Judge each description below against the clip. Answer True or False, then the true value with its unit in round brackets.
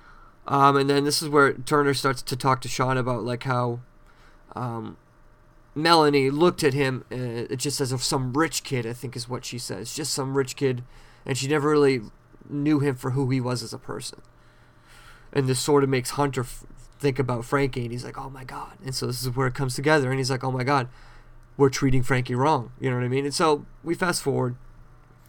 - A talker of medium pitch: False (130 Hz)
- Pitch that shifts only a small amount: True (2.2 semitones)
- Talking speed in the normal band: False (225 wpm)